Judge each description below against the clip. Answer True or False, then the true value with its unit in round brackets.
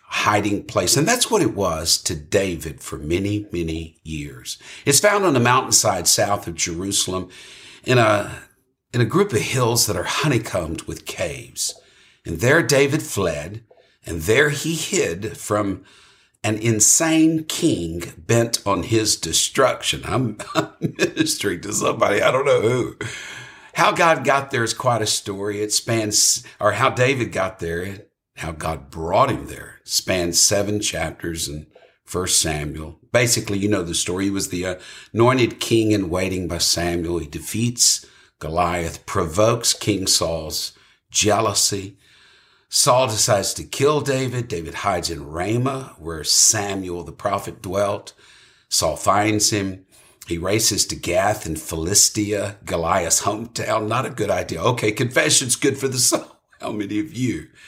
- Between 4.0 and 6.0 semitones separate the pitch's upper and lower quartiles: True (5.6 semitones)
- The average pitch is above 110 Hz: False (105 Hz)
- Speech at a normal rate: True (150 wpm)